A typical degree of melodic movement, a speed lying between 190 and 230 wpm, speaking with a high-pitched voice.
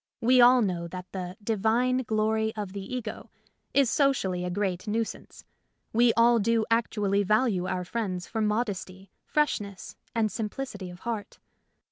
No: average, 3.5 semitones; average, 145 wpm; high, 215 Hz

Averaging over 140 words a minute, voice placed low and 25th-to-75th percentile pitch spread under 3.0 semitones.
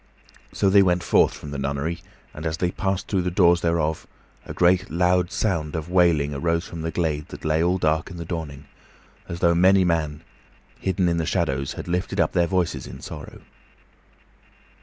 Yes: average, 190 wpm; very low, 85 Hz; narrow, 2.5 semitones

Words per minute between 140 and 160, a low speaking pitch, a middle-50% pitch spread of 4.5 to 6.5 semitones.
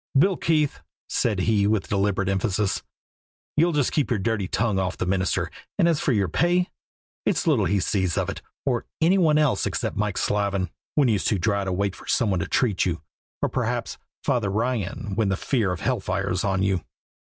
No: fast, 205 wpm; low, 105 Hz; average, 5.1 semitones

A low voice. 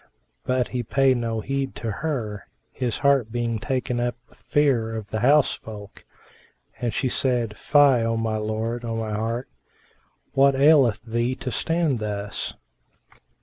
Yes: low, 120 Hz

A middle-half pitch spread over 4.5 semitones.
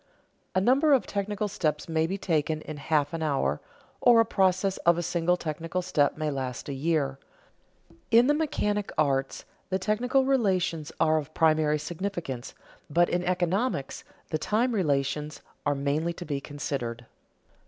Yes: average, 5.0 semitones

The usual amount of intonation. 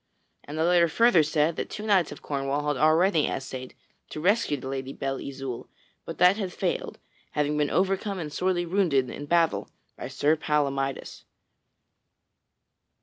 Yes: average, 4.6 semitones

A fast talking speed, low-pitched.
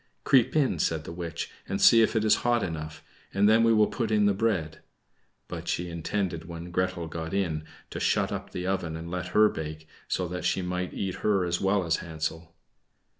Yes: fast, 210 wpm; very low, 90 Hz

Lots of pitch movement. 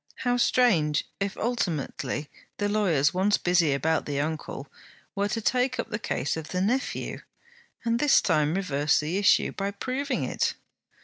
Yes: wide, 7.1 semitones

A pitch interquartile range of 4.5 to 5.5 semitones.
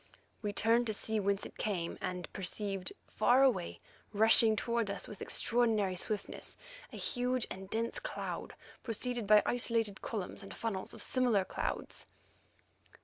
No: average, 3.0 semitones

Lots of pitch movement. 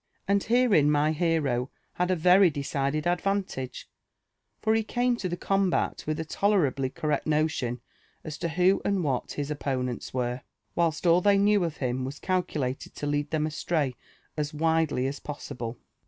No: average, 4.6 semitones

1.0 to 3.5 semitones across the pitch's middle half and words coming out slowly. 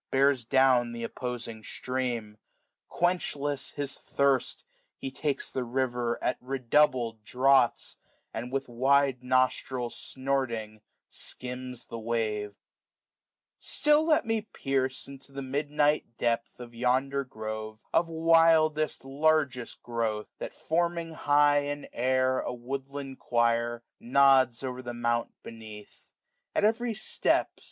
Yes: average, 3.2 semitones; slow, 115 wpm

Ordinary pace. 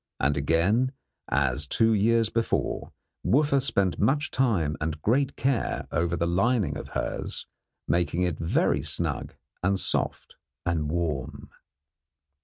No: slow, 125 wpm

